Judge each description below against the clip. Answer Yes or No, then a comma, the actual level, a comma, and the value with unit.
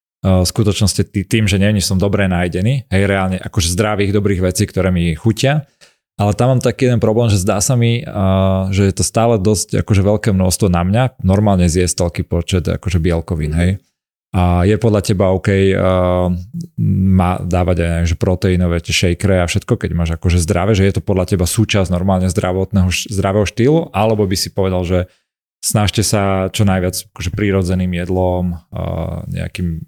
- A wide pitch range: No, narrow, 2.6 semitones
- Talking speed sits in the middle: No, fast, 175 wpm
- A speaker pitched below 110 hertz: Yes, very low, 95 Hz